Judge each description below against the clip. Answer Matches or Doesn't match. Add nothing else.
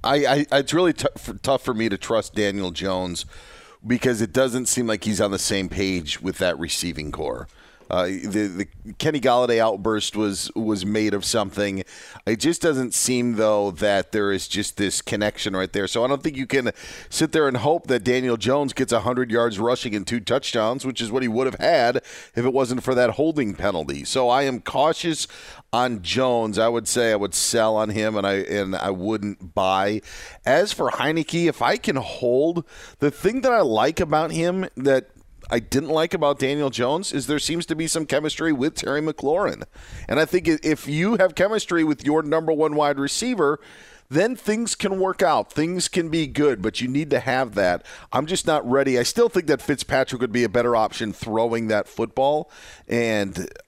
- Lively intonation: Matches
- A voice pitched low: Matches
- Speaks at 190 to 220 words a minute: Matches